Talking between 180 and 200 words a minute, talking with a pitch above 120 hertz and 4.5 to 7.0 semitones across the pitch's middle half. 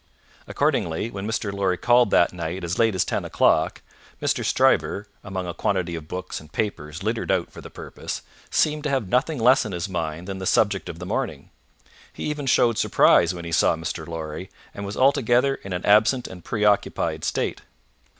No: average, 190 wpm; very low, 95 Hz; average, 5.0 semitones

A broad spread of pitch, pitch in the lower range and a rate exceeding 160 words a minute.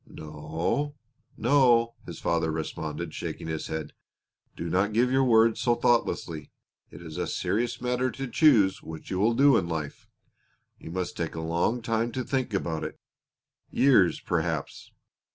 No: wide, 7.0 semitones; low, 105 Hz; average, 155 wpm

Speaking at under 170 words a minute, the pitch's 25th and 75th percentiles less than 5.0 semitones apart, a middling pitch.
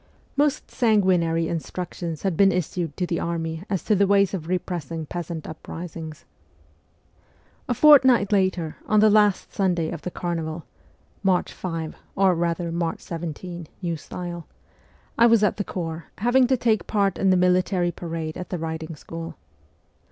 Yes: average, 155 wpm; average, 3.1 semitones; medium, 175 Hz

